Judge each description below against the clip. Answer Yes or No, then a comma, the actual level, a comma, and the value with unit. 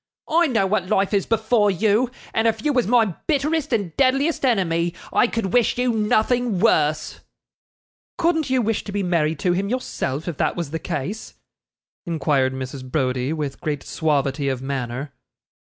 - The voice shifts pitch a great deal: Yes, wide, 7.9 semitones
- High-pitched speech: Yes, high, 195 Hz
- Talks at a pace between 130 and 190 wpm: Yes, average, 170 wpm